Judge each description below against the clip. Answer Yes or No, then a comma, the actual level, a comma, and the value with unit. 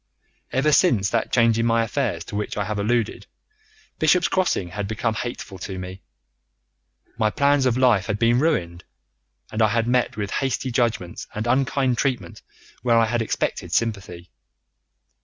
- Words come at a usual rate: Yes, average, 160 wpm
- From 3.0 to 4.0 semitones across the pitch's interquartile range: Yes, average, 3.7 semitones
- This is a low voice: Yes, low, 115 Hz